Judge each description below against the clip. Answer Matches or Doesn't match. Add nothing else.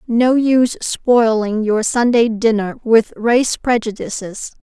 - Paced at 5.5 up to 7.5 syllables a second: Doesn't match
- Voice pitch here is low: Doesn't match